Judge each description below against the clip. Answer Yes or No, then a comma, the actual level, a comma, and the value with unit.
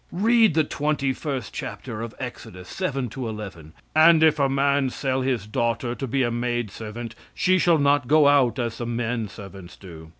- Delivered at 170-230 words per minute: Yes, average, 190 wpm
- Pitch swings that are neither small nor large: Yes, average, 4.1 semitones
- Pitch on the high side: No, low, 125 Hz